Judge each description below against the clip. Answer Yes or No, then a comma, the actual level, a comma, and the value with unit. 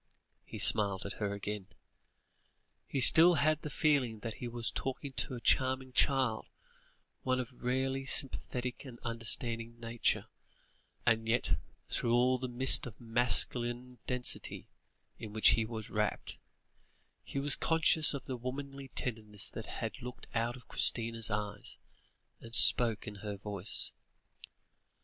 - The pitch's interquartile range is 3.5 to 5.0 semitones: No, average, 2.7 semitones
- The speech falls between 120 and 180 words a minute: Yes, average, 140 wpm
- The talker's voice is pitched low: Yes, low, 120 Hz